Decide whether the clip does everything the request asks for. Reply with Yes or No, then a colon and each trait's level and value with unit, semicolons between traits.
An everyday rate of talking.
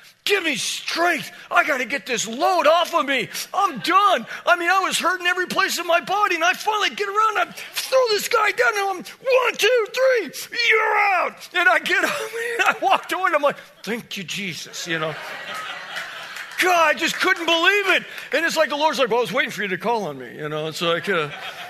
No: fast, 240 wpm